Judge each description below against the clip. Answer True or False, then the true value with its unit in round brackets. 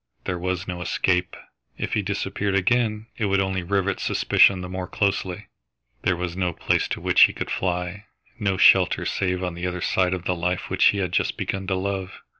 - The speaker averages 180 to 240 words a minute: True (205 wpm)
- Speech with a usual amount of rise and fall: False (1.5 semitones)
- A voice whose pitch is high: False (95 Hz)